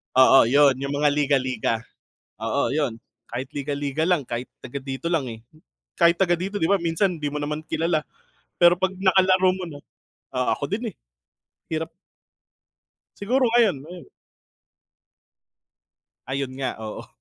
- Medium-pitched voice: Yes, medium, 150 Hz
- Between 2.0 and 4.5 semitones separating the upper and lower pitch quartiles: No, average, 4.9 semitones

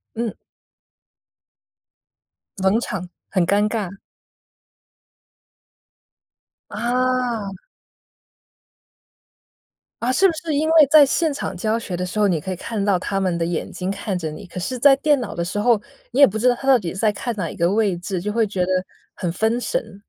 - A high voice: Yes, high, 210 Hz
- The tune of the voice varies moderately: Yes, average, 5.0 semitones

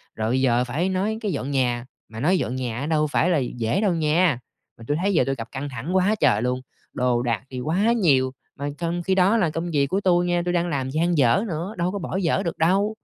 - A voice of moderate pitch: Yes, medium, 155 Hz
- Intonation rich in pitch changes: Yes, wide, 5.9 semitones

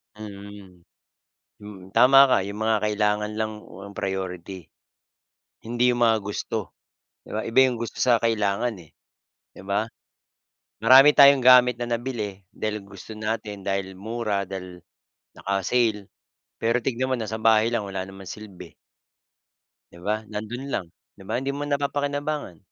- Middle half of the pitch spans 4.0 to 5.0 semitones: No, average, 3.5 semitones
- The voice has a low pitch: Yes, low, 110 Hz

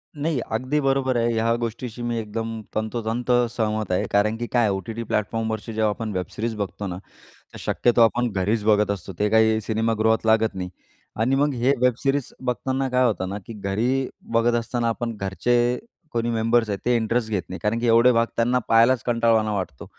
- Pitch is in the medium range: No, low, 115 Hz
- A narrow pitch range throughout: Yes, narrow, 2.0 semitones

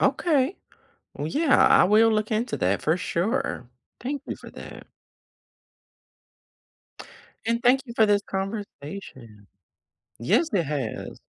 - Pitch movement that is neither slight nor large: No, wide, 7.7 semitones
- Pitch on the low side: No, high, 210 Hz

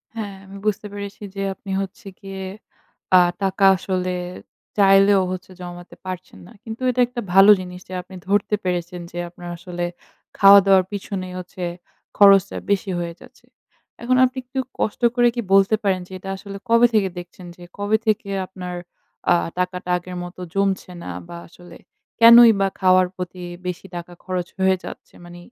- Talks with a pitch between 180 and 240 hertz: Yes, high, 190 Hz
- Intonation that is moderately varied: No, narrow, 1.9 semitones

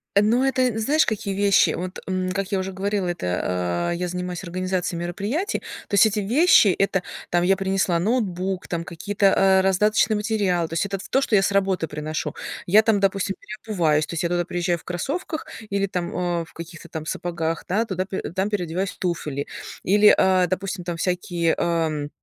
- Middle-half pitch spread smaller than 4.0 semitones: Yes, average, 2.8 semitones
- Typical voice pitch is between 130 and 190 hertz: Yes, medium, 185 Hz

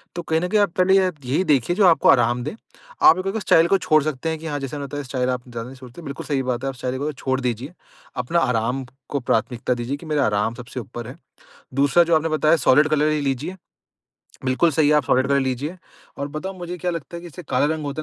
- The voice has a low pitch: No, medium, 145 Hz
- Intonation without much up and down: No, average, 4.3 semitones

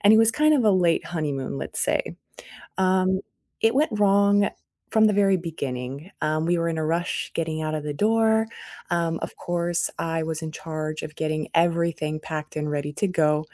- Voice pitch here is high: No, medium, 165 Hz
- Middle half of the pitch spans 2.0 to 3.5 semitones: No, average, 4.0 semitones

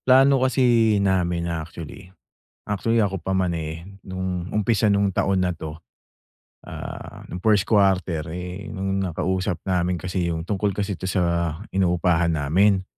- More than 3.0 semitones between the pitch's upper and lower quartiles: No, narrow, 2.6 semitones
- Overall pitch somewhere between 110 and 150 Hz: No, very low, 95 Hz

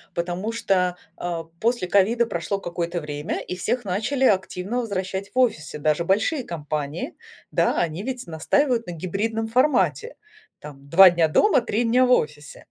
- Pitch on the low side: No, high, 190 Hz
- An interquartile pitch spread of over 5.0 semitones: Yes, wide, 5.6 semitones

